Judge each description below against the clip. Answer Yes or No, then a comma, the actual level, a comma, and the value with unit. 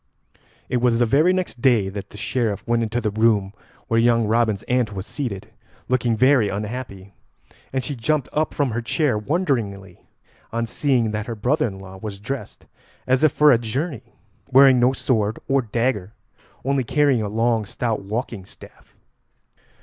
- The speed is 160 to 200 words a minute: Yes, average, 170 wpm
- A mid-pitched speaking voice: No, low, 115 Hz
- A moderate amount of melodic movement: Yes, average, 3.8 semitones